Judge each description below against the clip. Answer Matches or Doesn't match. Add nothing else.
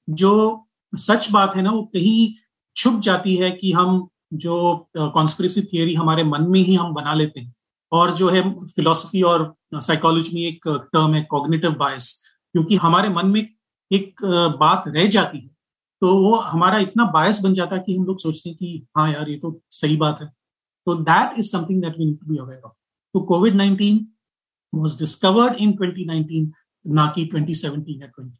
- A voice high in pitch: Doesn't match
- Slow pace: Doesn't match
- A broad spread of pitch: Doesn't match